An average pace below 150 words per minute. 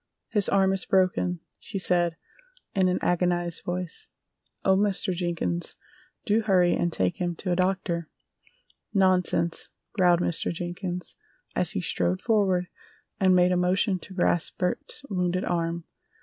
Yes: average, 140 wpm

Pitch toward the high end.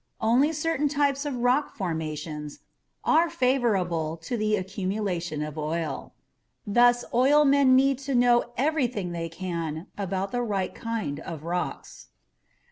Yes: high, 215 Hz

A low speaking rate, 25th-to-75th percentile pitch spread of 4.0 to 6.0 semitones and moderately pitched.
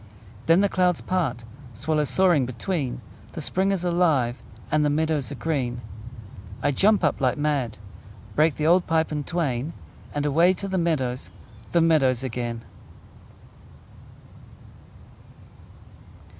Yes: slow, 130 wpm; average, 4.9 semitones; medium, 155 Hz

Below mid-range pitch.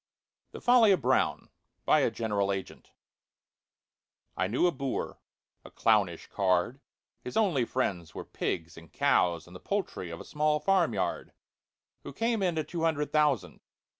Yes: low, 130 Hz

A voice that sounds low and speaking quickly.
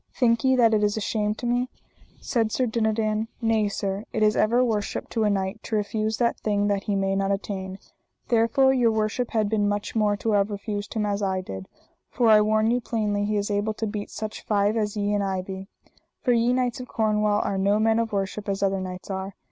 No: high, 210 Hz; fast, 235 wpm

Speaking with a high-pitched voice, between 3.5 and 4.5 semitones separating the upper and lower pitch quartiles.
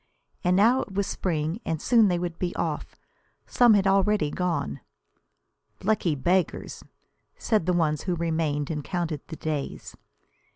No: medium, 175 Hz; average, 3.8 semitones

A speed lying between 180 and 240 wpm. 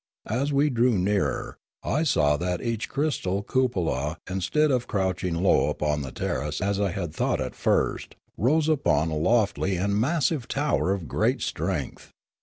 No: average, 165 wpm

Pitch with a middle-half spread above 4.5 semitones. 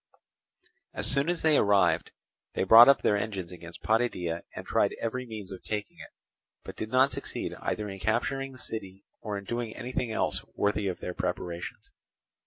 No: average, 4.2 semitones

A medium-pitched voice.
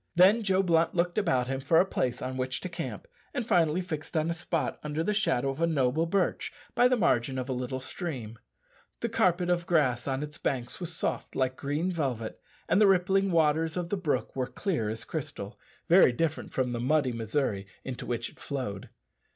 Yes: medium, 155 Hz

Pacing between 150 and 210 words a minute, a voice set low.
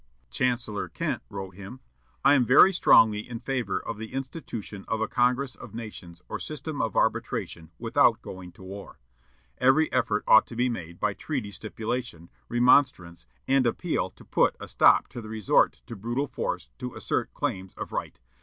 Yes: average, 175 wpm; low, 115 Hz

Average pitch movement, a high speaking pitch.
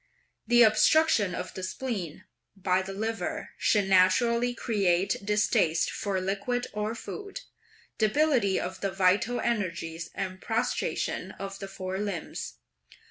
Yes: average, 3.8 semitones; high, 200 Hz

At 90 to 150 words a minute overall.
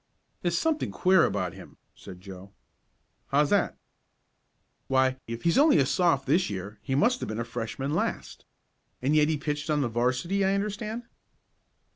No: average, 165 wpm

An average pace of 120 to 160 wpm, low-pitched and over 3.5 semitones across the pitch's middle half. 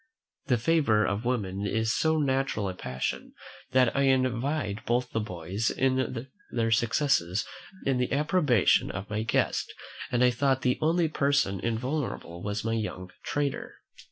Yes: average, 145 wpm; low, 120 Hz; average, 4.6 semitones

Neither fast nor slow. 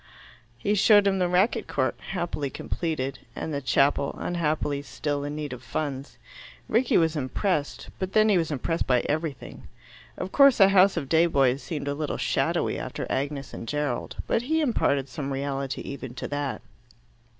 Yes: average, 170 wpm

